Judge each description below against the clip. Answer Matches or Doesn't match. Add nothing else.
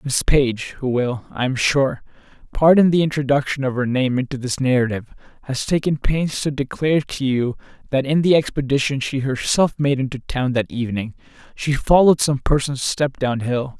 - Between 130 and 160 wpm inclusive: Doesn't match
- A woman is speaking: Doesn't match